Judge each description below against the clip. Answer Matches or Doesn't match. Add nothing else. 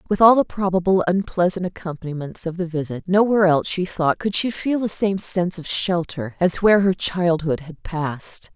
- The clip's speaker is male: Doesn't match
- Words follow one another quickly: Doesn't match